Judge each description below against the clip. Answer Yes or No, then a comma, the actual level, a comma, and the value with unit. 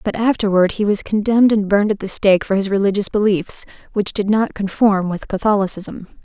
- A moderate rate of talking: Yes, average, 190 wpm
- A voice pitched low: No, high, 205 Hz